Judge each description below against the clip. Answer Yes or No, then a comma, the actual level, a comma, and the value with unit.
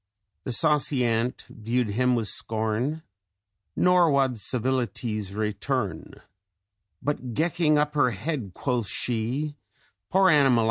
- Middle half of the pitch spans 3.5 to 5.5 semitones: Yes, average, 4.9 semitones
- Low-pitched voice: Yes, low, 125 Hz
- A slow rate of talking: Yes, slow, 110 wpm